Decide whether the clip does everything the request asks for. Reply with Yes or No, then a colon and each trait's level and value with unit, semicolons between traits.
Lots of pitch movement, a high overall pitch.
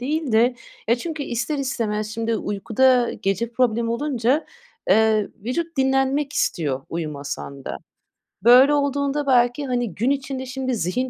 No: average, 3.7 semitones; very high, 250 Hz